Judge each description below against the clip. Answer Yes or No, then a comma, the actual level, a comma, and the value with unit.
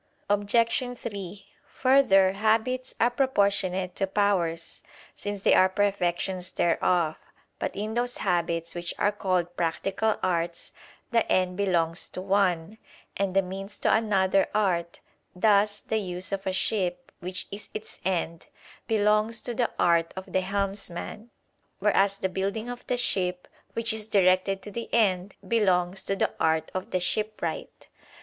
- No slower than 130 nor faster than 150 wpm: Yes, average, 145 wpm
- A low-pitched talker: No, high, 195 Hz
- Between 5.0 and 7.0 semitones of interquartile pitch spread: No, average, 2.8 semitones